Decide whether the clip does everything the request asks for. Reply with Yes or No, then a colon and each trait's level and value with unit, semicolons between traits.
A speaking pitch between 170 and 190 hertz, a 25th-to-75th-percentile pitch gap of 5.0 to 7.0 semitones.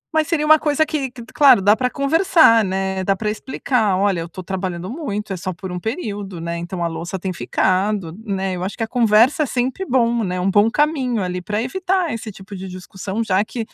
No: high, 210 Hz; average, 5.3 semitones